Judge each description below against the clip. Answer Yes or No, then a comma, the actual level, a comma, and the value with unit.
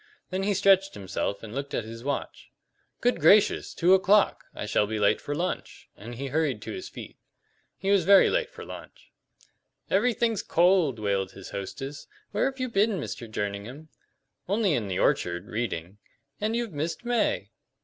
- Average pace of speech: Yes, average, 170 wpm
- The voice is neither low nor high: Yes, medium, 155 Hz